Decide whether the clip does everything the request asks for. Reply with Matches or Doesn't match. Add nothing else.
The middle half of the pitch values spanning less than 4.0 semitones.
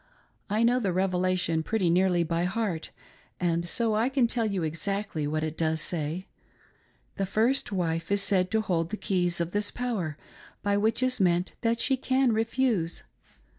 Doesn't match